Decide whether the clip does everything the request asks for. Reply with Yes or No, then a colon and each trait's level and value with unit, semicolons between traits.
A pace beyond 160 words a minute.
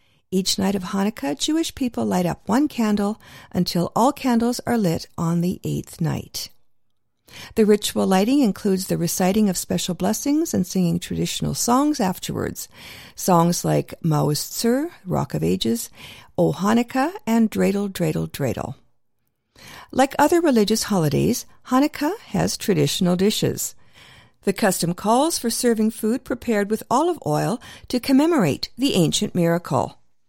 No: slow, 135 wpm